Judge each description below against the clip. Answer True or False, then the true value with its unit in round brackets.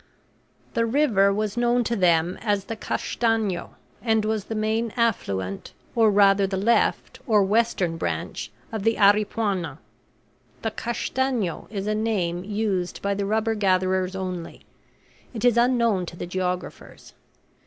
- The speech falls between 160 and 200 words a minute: False (140 wpm)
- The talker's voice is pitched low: False (205 Hz)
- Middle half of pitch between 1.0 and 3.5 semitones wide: True (3.2 semitones)